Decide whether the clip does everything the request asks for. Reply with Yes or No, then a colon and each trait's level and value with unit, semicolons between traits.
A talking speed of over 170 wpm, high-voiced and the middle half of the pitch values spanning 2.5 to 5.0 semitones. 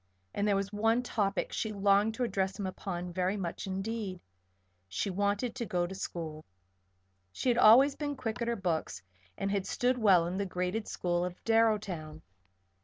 Yes: average, 180 wpm; high, 200 Hz; average, 3.7 semitones